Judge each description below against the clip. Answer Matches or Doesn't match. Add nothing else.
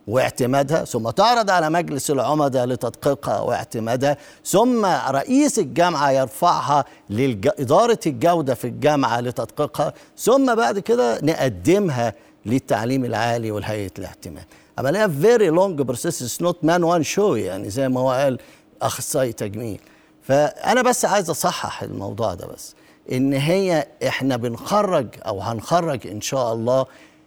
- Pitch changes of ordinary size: Doesn't match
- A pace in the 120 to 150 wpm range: Matches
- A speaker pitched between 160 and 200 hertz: Doesn't match